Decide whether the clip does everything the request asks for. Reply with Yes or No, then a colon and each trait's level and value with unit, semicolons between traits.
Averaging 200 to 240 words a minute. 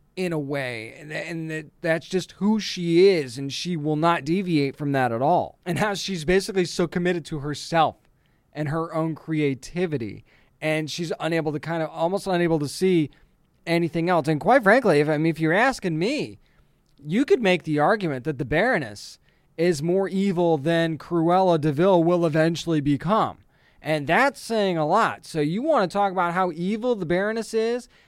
No: average, 185 wpm